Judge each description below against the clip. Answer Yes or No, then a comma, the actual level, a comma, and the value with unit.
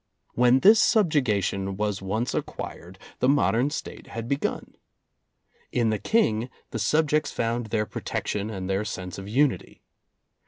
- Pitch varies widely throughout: Yes, wide, 5.7 semitones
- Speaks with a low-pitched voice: Yes, low, 115 Hz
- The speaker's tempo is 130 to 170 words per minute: Yes, average, 145 wpm